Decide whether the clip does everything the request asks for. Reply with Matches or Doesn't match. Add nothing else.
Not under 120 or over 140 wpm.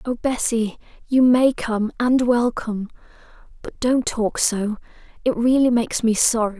Matches